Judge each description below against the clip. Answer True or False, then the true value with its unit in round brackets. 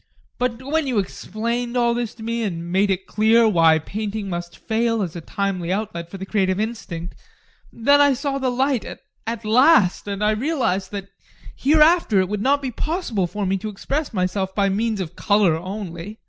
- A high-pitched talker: True (215 Hz)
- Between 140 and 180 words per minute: False (190 wpm)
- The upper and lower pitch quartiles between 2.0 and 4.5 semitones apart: True (4.2 semitones)